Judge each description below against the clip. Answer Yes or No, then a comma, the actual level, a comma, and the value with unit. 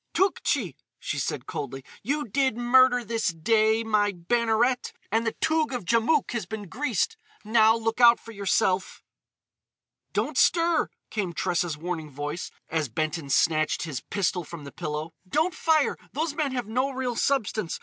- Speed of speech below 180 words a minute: Yes, average, 155 wpm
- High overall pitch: Yes, high, 220 Hz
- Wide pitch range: Yes, wide, 6.8 semitones